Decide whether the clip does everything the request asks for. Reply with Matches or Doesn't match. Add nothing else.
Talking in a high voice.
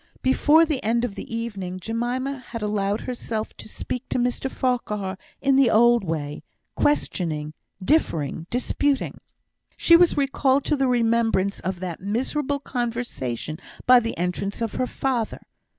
Matches